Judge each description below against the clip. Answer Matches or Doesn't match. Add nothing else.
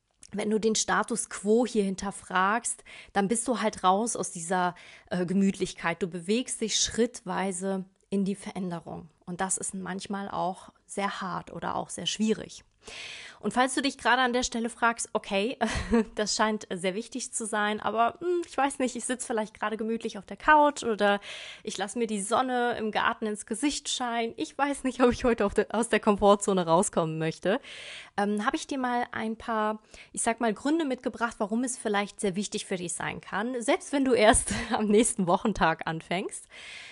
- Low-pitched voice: Doesn't match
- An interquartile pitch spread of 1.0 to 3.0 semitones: Doesn't match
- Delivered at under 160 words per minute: Doesn't match